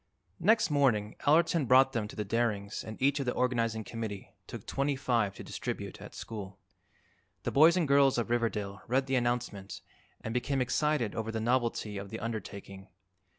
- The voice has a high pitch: No, low, 120 Hz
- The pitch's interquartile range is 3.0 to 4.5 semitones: Yes, average, 4.2 semitones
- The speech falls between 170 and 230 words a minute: Yes, average, 175 wpm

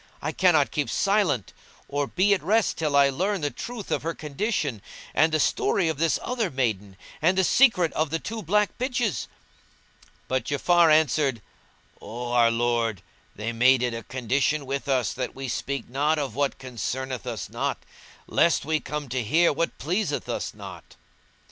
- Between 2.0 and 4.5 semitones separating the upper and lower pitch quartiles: No, average, 5.2 semitones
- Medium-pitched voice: Yes, medium, 145 Hz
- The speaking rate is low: No, average, 175 wpm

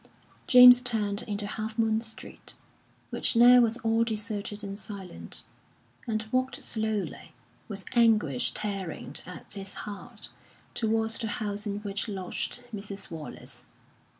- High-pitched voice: Yes, high, 215 Hz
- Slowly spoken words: Yes, slow, 125 wpm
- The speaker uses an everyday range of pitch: No, narrow, 2.0 semitones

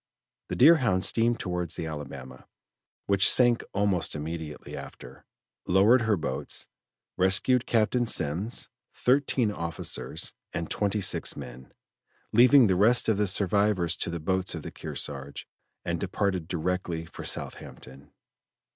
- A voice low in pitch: Yes, very low, 95 Hz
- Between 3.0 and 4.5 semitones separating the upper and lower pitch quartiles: No, average, 5.3 semitones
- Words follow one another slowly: Yes, slow, 130 wpm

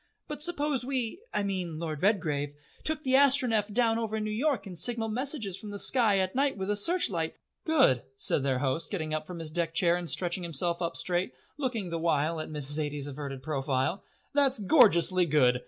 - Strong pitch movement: Yes, wide, 7.3 semitones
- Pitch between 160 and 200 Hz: Yes, medium, 185 Hz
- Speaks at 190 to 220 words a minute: Yes, average, 200 wpm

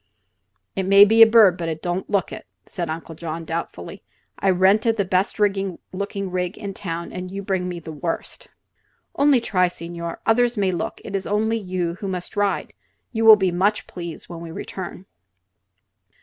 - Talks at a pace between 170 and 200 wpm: Yes, average, 180 wpm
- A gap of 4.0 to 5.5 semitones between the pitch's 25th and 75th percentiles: No, average, 2.9 semitones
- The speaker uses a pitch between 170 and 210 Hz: Yes, medium, 185 Hz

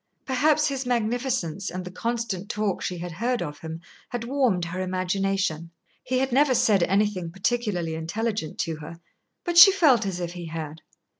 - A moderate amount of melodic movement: No, wide, 6.0 semitones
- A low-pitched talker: No, high, 195 Hz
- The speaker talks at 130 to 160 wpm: No, average, 170 wpm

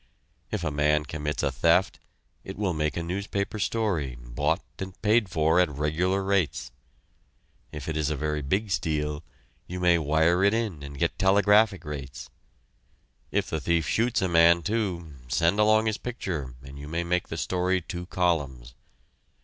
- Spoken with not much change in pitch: No, average, 4.3 semitones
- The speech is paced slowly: No, average, 165 wpm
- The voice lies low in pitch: Yes, very low, 85 Hz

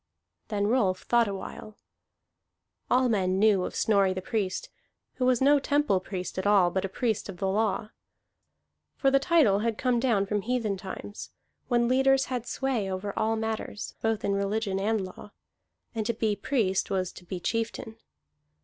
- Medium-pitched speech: No, high, 215 Hz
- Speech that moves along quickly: No, average, 170 wpm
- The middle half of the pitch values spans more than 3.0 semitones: Yes, average, 3.6 semitones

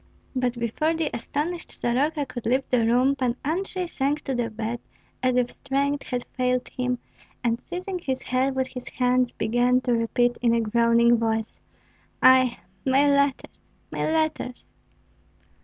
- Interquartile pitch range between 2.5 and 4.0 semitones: Yes, average, 2.8 semitones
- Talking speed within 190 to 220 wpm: No, average, 155 wpm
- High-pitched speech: Yes, very high, 255 Hz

